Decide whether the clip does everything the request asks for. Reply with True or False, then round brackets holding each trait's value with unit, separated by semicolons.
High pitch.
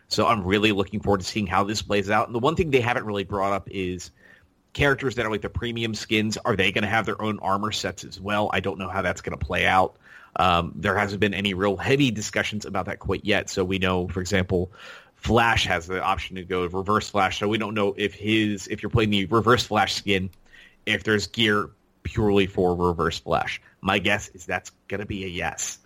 False (100 Hz)